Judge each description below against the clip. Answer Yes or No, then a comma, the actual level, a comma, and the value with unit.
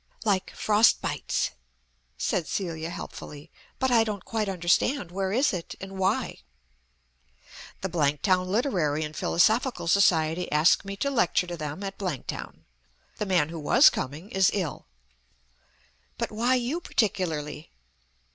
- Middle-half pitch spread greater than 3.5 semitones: Yes, average, 4.6 semitones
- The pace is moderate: No, slow, 130 wpm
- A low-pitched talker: No, medium, 185 Hz